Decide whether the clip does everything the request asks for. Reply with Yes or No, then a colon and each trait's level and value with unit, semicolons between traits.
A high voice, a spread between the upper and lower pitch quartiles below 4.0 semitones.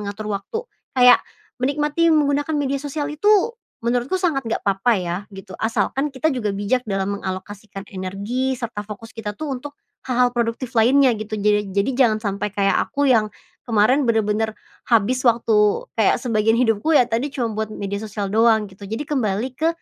No: high, 225 Hz; average, 4.3 semitones